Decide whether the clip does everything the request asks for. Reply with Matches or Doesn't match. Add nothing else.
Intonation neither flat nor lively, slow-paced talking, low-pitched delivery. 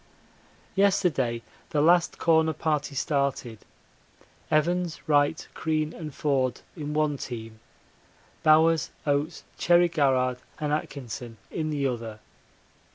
Doesn't match